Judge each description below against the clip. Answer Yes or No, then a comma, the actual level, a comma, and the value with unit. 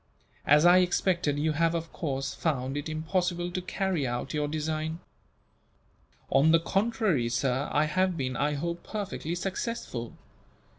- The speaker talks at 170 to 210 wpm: No, average, 145 wpm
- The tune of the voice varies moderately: Yes, average, 3.5 semitones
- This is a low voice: No, medium, 160 Hz